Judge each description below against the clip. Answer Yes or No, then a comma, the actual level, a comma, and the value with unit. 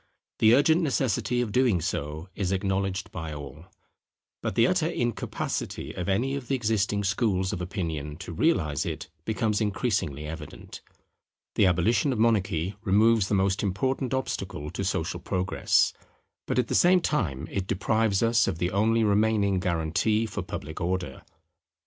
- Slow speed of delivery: No, average, 155 wpm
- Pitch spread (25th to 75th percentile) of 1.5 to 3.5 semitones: No, average, 4.2 semitones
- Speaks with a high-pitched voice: No, low, 100 Hz